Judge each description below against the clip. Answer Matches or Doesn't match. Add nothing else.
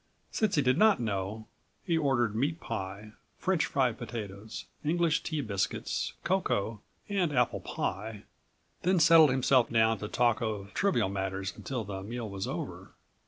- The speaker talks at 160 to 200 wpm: Doesn't match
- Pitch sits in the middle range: Doesn't match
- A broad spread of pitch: Matches